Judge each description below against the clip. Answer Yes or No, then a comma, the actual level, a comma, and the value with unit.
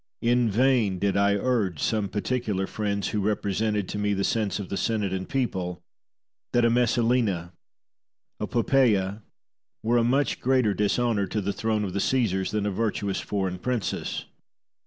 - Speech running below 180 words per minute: Yes, average, 165 wpm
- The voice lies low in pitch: Yes, low, 105 Hz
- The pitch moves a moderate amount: Yes, average, 3.2 semitones